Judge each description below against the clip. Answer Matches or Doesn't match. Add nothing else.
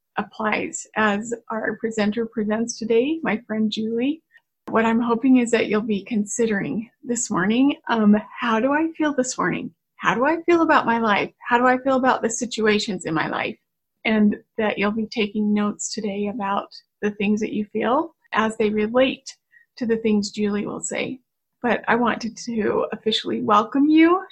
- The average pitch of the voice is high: Matches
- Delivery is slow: Doesn't match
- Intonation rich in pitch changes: Doesn't match